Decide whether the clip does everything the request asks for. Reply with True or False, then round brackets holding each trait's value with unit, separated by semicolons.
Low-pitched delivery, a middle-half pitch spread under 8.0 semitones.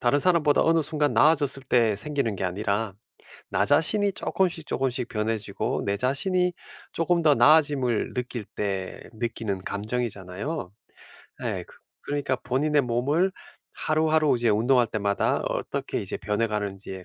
True (125 Hz; 6.1 semitones)